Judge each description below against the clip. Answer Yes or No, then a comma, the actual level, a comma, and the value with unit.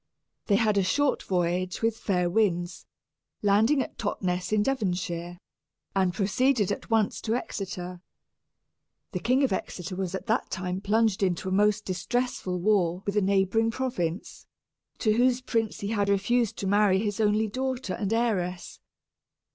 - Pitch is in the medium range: No, high, 200 Hz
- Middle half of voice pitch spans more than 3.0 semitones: Yes, average, 3.5 semitones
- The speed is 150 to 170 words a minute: Yes, average, 155 wpm